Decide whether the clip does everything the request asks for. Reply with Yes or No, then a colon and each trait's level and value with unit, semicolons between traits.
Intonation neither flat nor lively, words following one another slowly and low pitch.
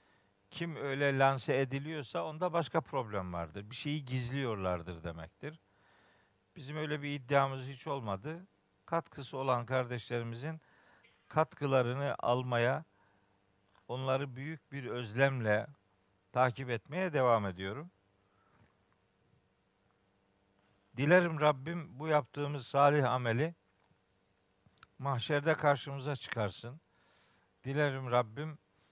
No: wide, 6.5 semitones; slow, 85 wpm; low, 130 Hz